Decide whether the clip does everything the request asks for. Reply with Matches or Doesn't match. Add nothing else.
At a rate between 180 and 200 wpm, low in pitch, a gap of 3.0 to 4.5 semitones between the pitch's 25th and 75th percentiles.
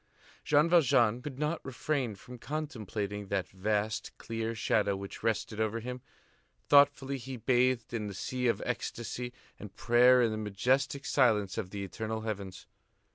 Doesn't match